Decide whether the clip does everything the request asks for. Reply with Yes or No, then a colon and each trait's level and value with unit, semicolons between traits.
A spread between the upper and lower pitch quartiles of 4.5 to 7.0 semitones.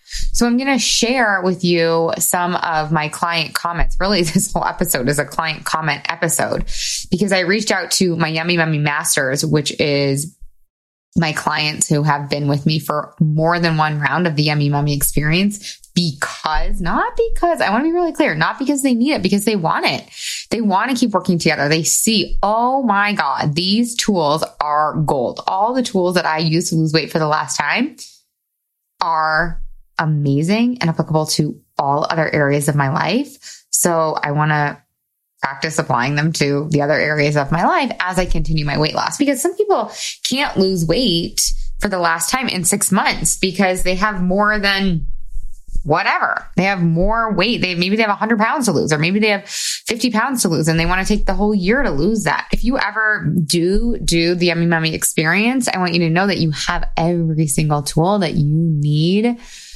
Yes: average, 5.0 semitones